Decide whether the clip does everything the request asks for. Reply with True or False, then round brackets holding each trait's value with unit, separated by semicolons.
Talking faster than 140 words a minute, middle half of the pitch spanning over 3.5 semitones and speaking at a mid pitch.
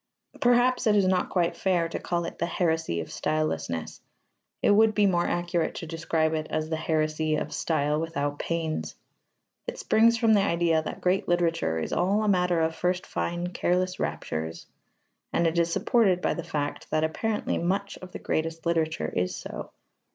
False (180 wpm; 2.7 semitones; 170 Hz)